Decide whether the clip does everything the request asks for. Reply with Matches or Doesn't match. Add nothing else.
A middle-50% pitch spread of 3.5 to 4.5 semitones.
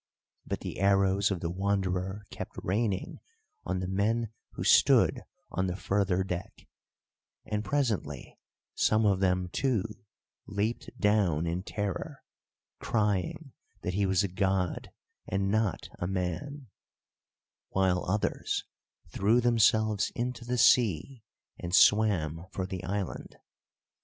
Doesn't match